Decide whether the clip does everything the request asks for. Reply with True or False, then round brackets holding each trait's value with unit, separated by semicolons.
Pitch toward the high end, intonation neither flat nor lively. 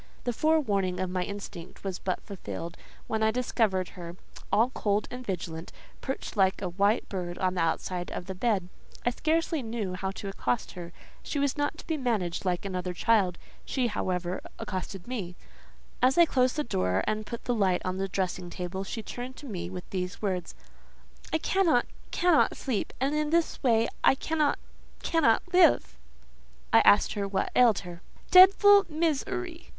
False (205 Hz; 6.4 semitones)